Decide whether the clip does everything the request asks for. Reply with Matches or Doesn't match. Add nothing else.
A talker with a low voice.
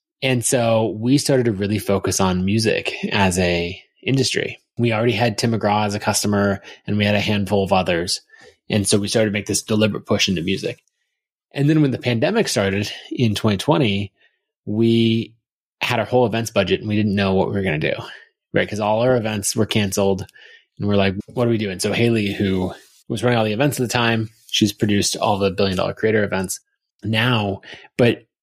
Matches